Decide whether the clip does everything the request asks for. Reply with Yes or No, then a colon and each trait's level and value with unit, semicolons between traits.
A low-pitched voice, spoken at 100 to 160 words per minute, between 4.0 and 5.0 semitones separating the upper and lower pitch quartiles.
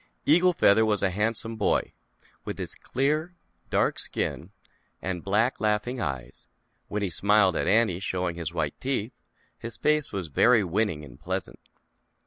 Yes: low, 105 Hz; average, 150 wpm; average, 4.6 semitones